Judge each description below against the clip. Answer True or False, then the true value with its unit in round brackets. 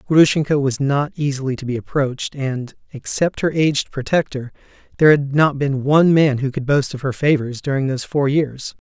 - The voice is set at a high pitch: False (140 Hz)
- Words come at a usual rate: True (190 wpm)